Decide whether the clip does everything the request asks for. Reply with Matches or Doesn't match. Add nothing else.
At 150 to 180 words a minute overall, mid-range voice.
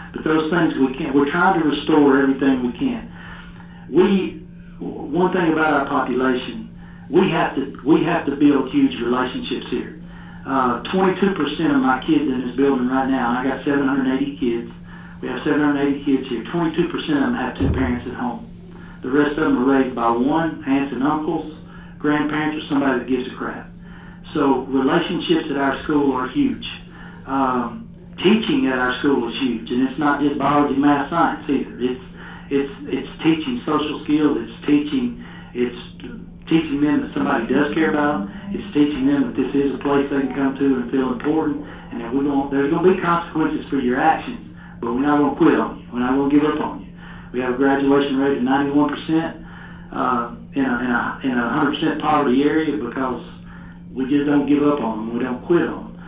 Doesn't match